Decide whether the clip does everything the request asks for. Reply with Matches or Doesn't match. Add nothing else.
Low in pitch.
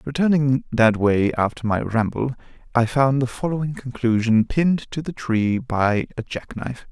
Matches